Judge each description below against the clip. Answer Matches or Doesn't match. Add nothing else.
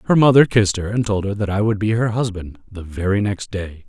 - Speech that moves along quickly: Matches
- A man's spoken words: Matches